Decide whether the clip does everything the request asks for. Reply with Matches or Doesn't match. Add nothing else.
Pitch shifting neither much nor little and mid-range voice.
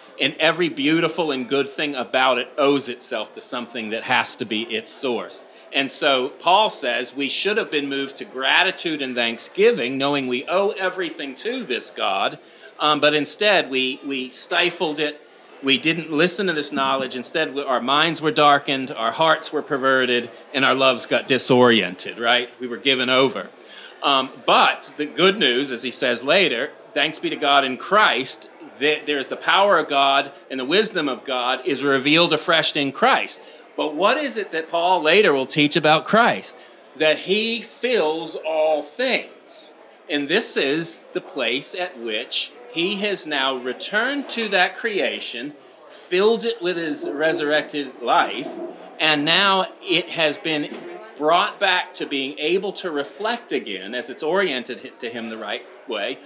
Matches